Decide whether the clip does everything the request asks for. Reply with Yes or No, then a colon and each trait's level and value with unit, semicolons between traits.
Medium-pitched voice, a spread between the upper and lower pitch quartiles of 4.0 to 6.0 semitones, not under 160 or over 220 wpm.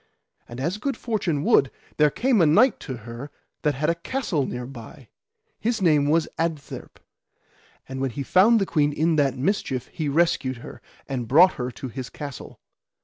Yes: medium, 150 Hz; average, 4.6 semitones; average, 180 wpm